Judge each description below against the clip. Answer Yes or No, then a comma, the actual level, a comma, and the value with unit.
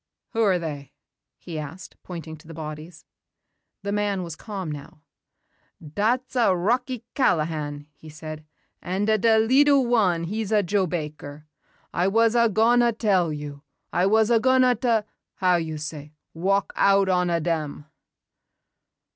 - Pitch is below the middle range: No, medium, 185 Hz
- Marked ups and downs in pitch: Yes, wide, 5.8 semitones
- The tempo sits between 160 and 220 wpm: No, average, 150 wpm